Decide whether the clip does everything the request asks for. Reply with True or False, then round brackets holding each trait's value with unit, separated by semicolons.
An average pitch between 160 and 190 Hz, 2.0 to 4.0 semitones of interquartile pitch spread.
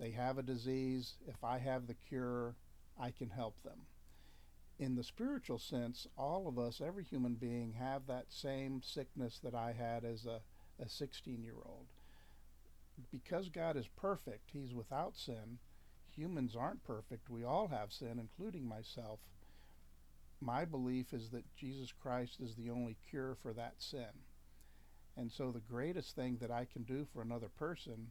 False (120 Hz; 3.0 semitones)